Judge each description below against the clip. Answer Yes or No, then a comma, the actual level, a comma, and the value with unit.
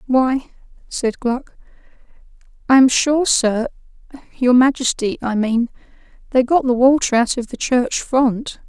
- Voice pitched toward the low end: No, very high, 250 Hz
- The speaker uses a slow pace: Yes, slow, 125 wpm